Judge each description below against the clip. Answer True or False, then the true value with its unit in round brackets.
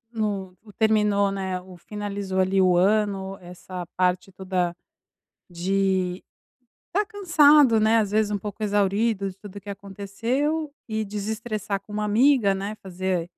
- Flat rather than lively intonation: True (2.3 semitones)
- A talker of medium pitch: False (200 Hz)